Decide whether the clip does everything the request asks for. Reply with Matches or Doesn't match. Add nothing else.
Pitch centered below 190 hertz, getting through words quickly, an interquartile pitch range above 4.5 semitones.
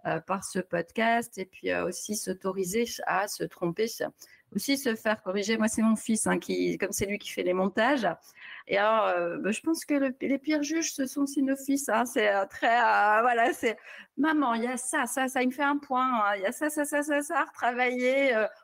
Doesn't match